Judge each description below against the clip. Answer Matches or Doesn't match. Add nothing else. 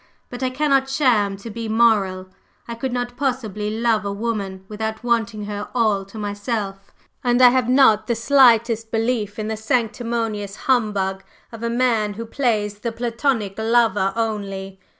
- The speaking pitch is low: Doesn't match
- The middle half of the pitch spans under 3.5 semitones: Matches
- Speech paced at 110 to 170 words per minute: Matches